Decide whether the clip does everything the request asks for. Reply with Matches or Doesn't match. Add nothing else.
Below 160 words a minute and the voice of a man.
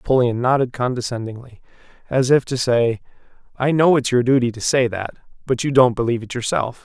Doesn't match